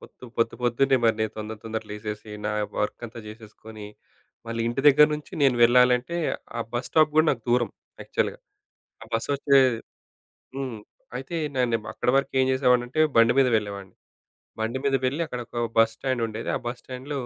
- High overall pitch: No, low, 120 Hz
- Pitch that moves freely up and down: No, average, 3.1 semitones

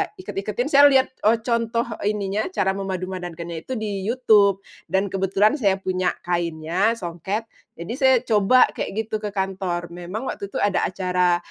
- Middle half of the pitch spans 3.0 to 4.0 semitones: Yes, average, 3.3 semitones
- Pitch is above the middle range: Yes, high, 195 Hz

